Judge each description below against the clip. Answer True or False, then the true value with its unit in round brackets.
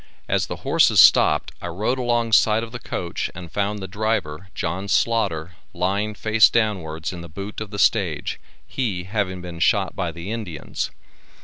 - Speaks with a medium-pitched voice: False (100 Hz)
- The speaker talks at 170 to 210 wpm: True (175 wpm)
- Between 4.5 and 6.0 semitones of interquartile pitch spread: False (4.0 semitones)